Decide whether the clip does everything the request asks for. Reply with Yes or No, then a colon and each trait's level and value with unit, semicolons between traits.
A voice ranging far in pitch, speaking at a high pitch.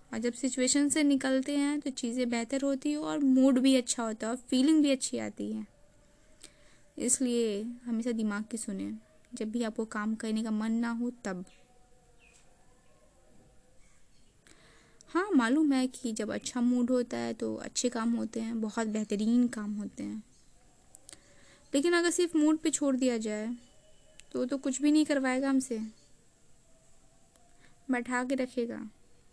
No: average, 3.3 semitones; high, 245 Hz